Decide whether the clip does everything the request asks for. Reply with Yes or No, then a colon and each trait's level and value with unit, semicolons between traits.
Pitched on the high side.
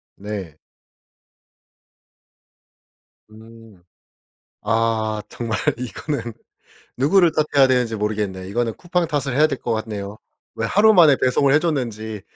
No: low, 115 Hz